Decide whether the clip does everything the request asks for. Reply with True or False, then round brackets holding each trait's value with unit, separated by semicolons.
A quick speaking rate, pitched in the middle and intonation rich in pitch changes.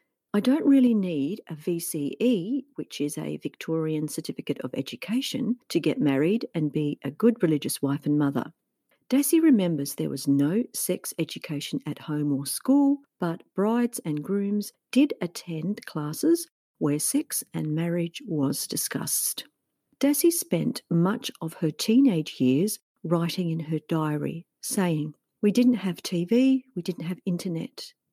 False (145 wpm; 175 Hz; 7.9 semitones)